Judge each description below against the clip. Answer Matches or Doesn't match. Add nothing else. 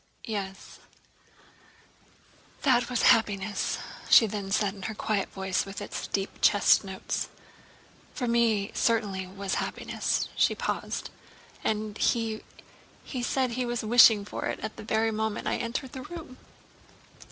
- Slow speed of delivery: Doesn't match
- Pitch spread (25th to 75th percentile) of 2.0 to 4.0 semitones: Matches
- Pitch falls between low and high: Doesn't match